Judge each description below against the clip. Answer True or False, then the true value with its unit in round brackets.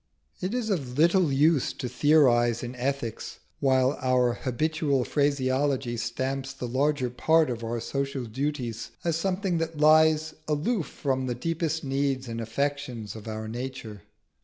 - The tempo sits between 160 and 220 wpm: False (145 wpm)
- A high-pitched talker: False (135 Hz)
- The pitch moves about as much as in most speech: True (3.9 semitones)